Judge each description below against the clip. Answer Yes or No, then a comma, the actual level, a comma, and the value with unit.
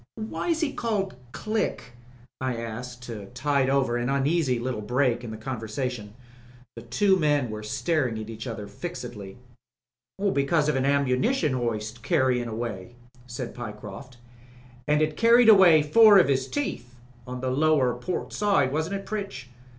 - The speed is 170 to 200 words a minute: No, average, 160 wpm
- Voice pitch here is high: No, low, 130 Hz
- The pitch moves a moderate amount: Yes, average, 4.8 semitones